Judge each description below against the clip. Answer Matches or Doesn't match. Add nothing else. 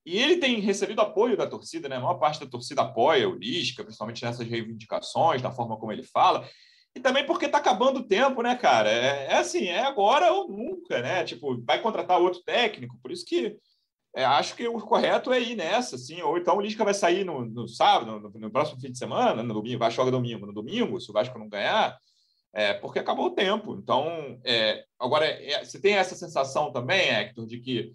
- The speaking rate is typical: Doesn't match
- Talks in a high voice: Matches